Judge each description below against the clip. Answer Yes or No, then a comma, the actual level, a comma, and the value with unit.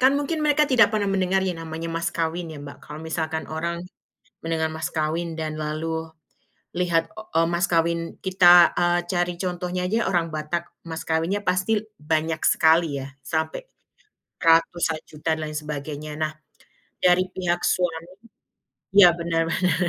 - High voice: No, medium, 170 Hz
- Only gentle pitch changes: Yes, narrow, 2.2 semitones